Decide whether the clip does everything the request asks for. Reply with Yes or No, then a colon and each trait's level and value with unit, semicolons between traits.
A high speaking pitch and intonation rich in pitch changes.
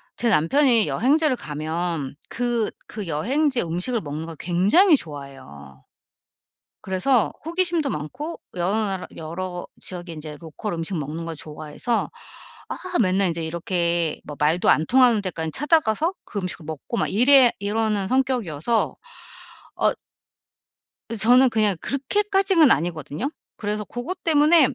Yes: high, 200 Hz; wide, 7.9 semitones